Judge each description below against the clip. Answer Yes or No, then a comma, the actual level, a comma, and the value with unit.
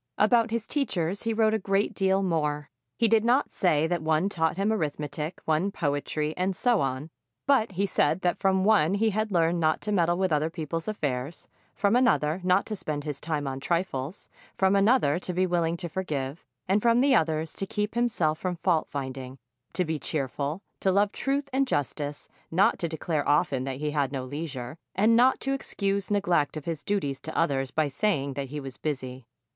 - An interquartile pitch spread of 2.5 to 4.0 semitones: No, average, 5.3 semitones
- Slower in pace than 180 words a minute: No, average, 200 wpm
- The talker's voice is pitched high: No, medium, 170 Hz